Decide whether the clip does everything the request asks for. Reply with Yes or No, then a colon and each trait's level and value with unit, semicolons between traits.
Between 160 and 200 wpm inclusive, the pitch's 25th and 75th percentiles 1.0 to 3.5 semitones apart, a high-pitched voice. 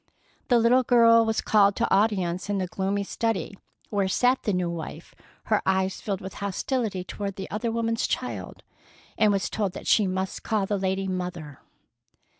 Yes: average, 175 wpm; average, 2.9 semitones; high, 200 Hz